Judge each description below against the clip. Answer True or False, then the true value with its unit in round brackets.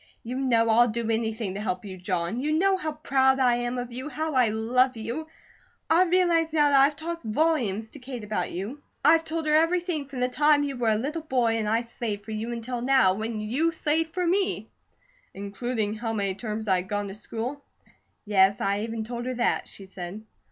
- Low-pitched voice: False (240 Hz)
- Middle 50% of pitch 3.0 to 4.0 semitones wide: False (5.6 semitones)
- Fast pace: True (210 wpm)